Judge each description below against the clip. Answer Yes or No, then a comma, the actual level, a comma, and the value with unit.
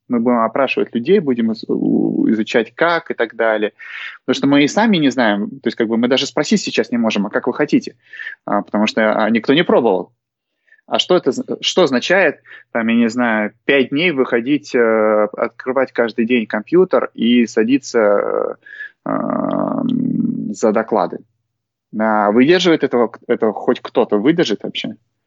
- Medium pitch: No, low, 120 Hz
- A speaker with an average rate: Yes, average, 150 wpm